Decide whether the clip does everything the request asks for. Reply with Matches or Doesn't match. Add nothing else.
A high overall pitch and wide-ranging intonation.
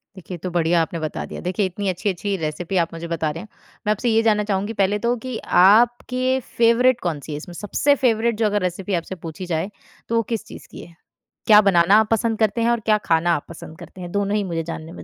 Doesn't match